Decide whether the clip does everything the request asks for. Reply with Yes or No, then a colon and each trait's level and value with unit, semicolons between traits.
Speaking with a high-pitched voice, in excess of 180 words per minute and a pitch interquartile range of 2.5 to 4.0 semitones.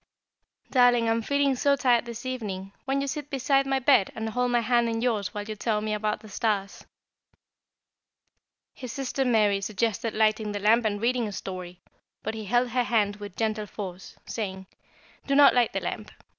Yes: high, 225 Hz; average, 190 wpm; average, 3.1 semitones